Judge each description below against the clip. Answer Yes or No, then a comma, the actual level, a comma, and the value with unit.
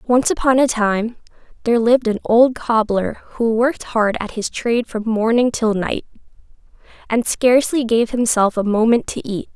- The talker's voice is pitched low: No, high, 230 Hz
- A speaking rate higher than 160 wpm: Yes, average, 170 wpm